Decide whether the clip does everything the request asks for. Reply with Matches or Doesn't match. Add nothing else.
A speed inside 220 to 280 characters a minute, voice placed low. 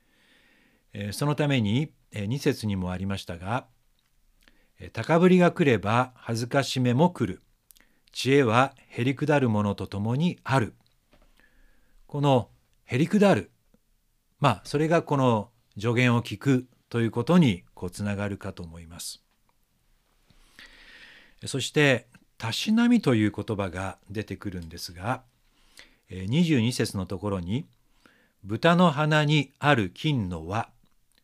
Matches